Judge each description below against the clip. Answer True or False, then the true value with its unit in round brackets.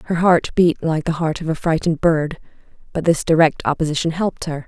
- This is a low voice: False (160 Hz)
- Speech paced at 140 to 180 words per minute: False (205 wpm)